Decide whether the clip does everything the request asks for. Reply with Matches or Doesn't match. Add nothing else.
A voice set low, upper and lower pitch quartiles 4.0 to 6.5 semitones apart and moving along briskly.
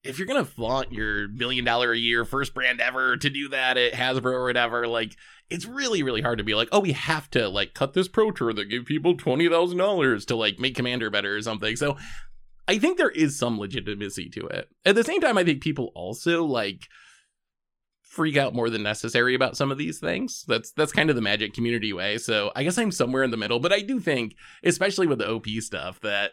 Matches